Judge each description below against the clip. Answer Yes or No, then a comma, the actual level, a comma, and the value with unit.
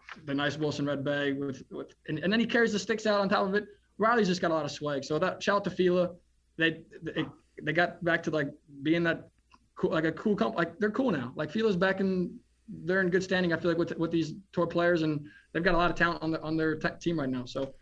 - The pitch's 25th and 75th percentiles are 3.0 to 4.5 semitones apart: Yes, average, 3.7 semitones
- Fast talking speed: Yes, fast, 275 wpm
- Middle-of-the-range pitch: Yes, medium, 170 Hz